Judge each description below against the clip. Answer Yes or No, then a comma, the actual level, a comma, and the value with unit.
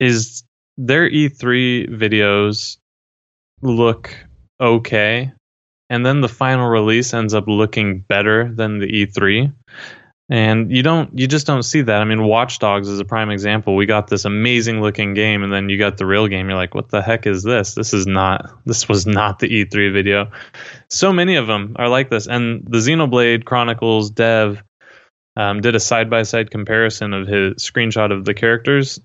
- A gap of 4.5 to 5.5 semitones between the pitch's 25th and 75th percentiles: No, average, 2.9 semitones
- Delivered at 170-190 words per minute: Yes, average, 180 wpm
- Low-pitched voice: Yes, low, 110 Hz